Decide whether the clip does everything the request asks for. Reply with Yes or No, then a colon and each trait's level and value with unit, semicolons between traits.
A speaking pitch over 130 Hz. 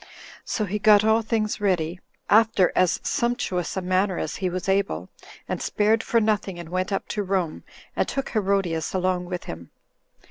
Yes: high, 190 Hz